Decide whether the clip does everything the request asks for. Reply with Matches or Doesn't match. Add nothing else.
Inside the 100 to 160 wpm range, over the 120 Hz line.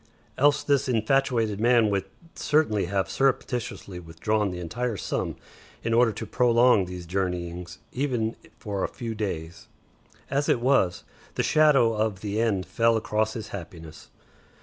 Doesn't match